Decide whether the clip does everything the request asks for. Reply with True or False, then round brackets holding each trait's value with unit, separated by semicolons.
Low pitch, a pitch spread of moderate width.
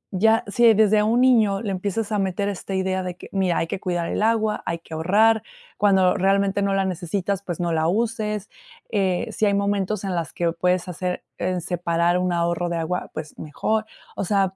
False (190 Hz; 3.0 semitones)